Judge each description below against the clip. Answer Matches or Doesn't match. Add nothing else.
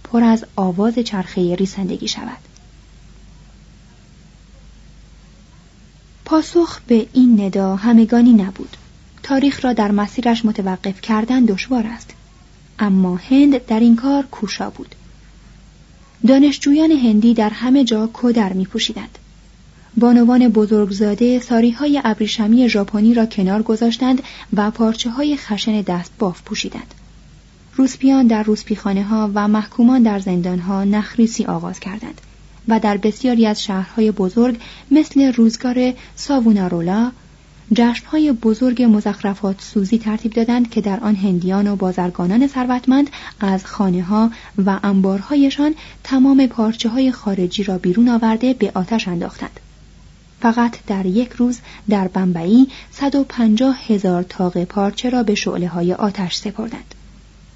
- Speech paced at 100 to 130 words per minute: Matches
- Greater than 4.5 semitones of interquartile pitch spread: Doesn't match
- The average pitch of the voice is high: Matches